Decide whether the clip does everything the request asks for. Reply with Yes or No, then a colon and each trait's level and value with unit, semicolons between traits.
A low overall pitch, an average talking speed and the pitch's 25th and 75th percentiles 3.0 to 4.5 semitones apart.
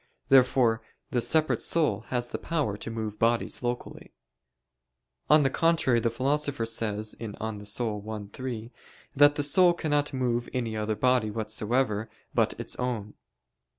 Yes: low, 120 Hz; average, 145 wpm; average, 3.7 semitones